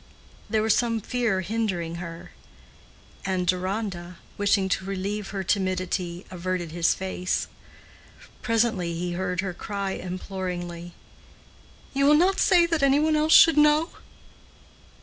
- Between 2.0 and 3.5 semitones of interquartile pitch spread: No, average, 4.2 semitones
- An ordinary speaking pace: No, slow, 130 wpm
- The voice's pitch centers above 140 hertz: Yes, high, 190 Hz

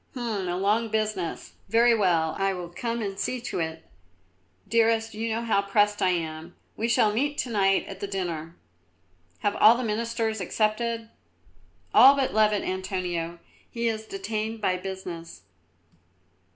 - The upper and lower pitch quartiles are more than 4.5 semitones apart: No, average, 3.7 semitones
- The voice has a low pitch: No, high, 210 Hz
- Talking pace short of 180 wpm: Yes, average, 150 wpm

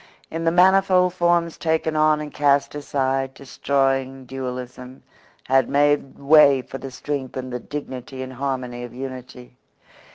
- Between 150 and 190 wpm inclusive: No, average, 140 wpm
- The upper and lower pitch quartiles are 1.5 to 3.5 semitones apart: Yes, average, 2.8 semitones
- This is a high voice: No, low, 135 Hz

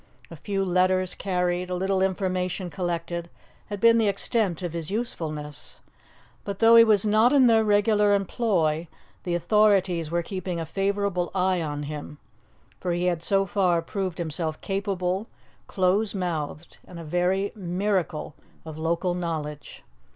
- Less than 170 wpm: Yes, average, 150 wpm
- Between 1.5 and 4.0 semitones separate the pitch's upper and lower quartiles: Yes, average, 2.9 semitones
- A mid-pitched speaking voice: Yes, medium, 180 Hz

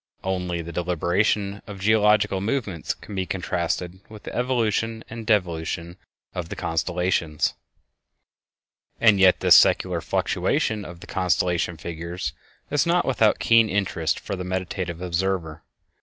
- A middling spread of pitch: Yes, average, 3.5 semitones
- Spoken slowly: Yes, slow, 130 wpm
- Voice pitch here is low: Yes, very low, 95 Hz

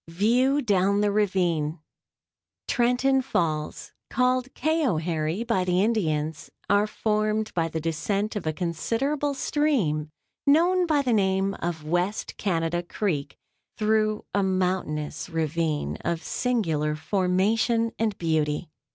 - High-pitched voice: Yes, high, 195 Hz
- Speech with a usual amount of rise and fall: No, wide, 5.9 semitones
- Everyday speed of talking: No, slow, 115 wpm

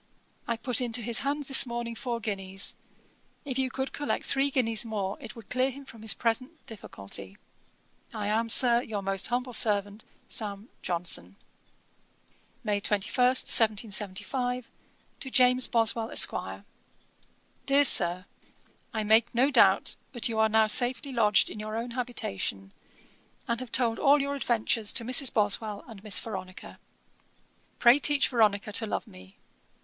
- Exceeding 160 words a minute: No, average, 150 wpm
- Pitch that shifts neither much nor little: Yes, average, 3.3 semitones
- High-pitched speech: Yes, high, 230 Hz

